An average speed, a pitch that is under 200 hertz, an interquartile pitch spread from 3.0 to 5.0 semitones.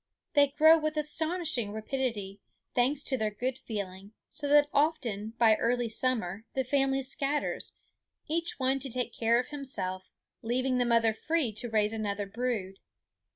No: average, 155 wpm; high, 245 Hz; average, 4.6 semitones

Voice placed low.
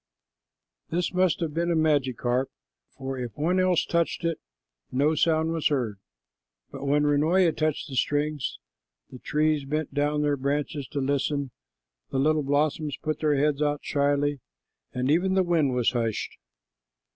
No: medium, 145 Hz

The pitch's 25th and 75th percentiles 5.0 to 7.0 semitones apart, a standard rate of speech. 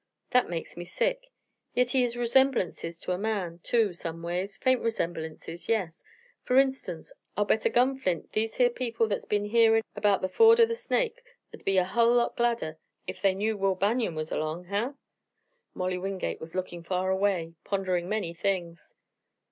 Yes: average, 5.3 semitones; average, 180 wpm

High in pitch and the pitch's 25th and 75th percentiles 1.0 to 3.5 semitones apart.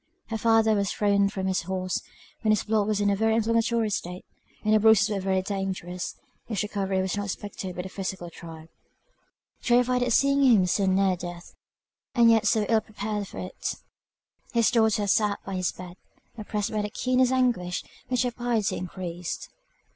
Yes: high, 205 Hz; average, 3.0 semitones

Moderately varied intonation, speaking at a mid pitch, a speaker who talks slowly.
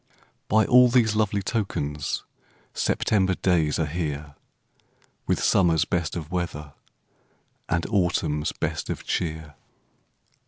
No: average, 4.8 semitones; very low, 85 Hz; slow, 110 wpm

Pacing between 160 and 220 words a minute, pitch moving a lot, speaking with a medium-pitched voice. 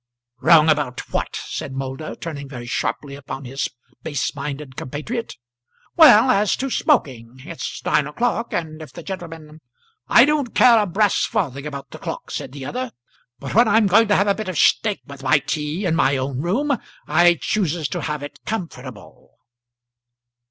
Yes: average, 175 wpm; wide, 7.2 semitones; medium, 160 Hz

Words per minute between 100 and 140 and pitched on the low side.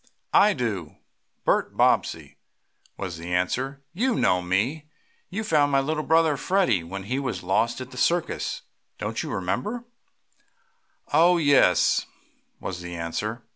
Yes: slow, 135 wpm; low, 130 Hz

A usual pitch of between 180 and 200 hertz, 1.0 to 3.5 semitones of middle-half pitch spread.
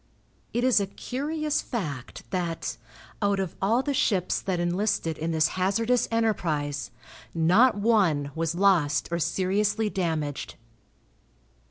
No: high, 190 Hz; average, 5.2 semitones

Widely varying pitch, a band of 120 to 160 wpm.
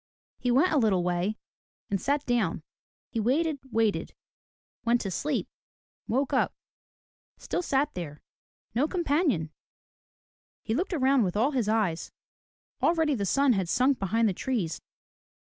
Yes: wide, 6.1 semitones; average, 150 wpm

